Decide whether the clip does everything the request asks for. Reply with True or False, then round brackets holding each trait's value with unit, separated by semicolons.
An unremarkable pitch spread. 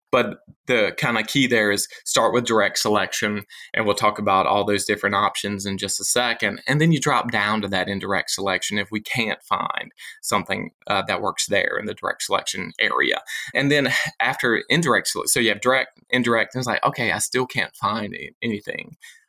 True (3.5 semitones)